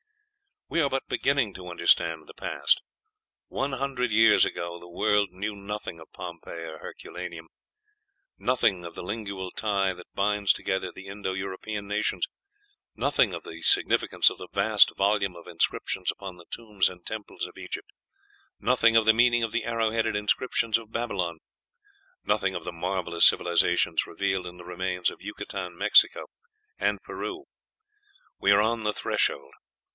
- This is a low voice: Yes, low, 100 Hz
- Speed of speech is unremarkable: Yes, average, 160 wpm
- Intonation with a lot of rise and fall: No, average, 3.8 semitones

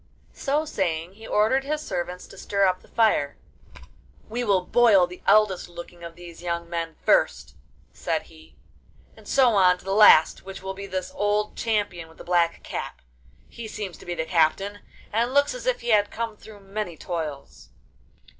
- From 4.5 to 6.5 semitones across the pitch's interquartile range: No, average, 4.0 semitones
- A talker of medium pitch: No, high, 195 Hz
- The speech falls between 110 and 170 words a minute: No, average, 185 wpm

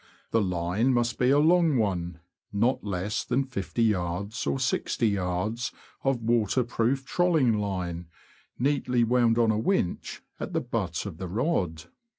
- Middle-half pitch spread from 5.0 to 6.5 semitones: Yes, wide, 5.4 semitones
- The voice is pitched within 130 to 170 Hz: No, low, 115 Hz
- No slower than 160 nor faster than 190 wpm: No, average, 145 wpm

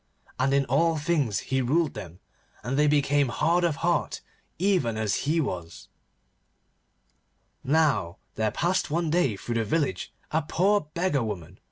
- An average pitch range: No, wide, 6.4 semitones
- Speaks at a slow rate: No, average, 150 wpm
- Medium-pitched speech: Yes, medium, 145 Hz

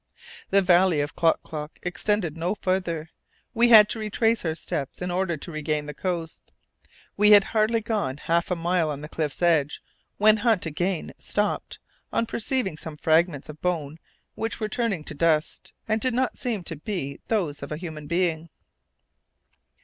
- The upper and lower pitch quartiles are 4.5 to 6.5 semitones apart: Yes, average, 5.1 semitones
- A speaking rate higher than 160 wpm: Yes, average, 170 wpm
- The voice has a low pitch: No, medium, 175 Hz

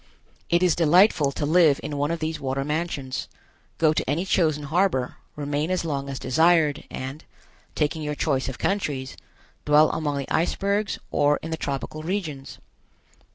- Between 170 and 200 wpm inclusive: No, average, 160 wpm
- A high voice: No, medium, 150 Hz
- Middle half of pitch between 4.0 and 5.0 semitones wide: No, average, 3.0 semitones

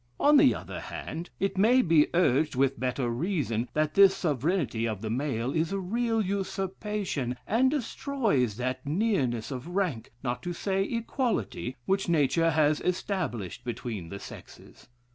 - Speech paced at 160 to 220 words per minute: No, average, 150 wpm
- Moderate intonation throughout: No, wide, 7.7 semitones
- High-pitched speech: No, medium, 160 Hz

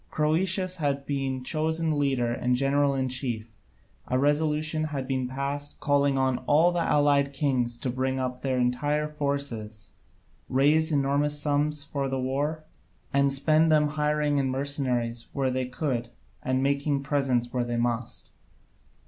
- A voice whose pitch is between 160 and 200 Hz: No, medium, 140 Hz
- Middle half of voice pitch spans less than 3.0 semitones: Yes, narrow, 2.5 semitones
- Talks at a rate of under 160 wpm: Yes, average, 150 wpm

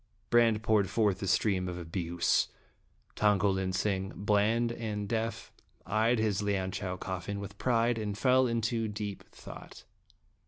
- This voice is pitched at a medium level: No, low, 105 Hz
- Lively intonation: No, average, 2.9 semitones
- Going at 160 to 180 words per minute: No, average, 145 wpm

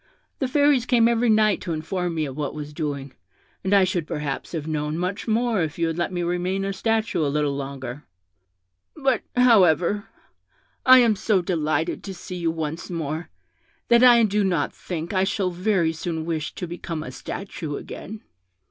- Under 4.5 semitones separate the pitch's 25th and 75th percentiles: No, average, 5.1 semitones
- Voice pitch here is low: No, medium, 175 Hz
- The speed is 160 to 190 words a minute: Yes, average, 185 wpm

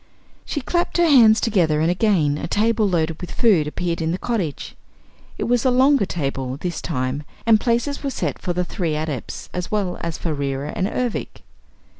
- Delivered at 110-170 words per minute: No, average, 190 wpm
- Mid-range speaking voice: Yes, medium, 180 Hz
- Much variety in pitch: Yes, wide, 6.8 semitones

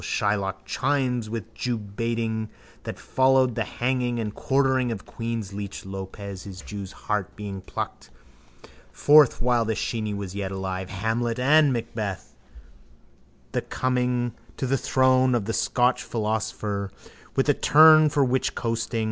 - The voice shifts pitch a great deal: No, average, 4.1 semitones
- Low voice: Yes, low, 115 Hz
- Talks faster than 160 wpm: No, average, 145 wpm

